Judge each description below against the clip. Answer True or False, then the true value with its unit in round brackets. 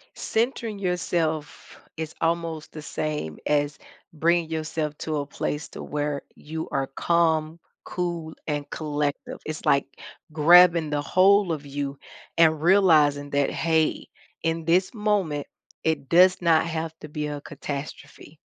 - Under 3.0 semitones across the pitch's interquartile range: True (2.4 semitones)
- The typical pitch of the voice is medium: True (160 Hz)